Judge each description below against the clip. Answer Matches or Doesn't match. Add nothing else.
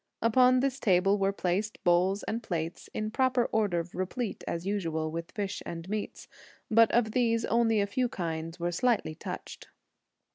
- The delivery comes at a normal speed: Matches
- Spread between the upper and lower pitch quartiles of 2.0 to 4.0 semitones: Doesn't match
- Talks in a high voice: Matches